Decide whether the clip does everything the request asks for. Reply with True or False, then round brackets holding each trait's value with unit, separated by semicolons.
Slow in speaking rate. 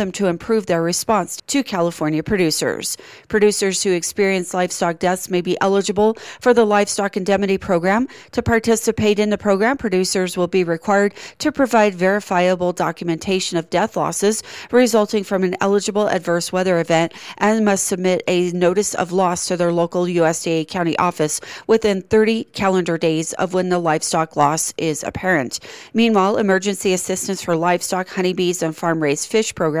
False (155 wpm)